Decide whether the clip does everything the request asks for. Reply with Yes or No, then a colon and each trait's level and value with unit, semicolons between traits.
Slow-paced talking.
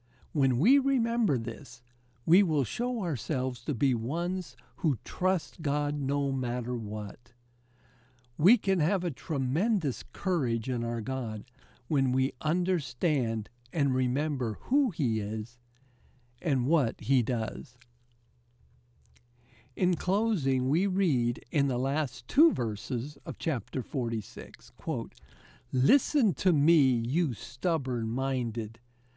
Yes: slow, 115 wpm